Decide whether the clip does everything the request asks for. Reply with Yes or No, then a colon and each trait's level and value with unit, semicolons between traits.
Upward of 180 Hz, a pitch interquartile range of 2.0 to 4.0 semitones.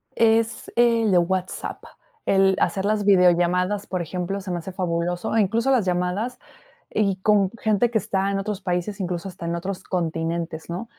Yes: high, 190 Hz; average, 2.8 semitones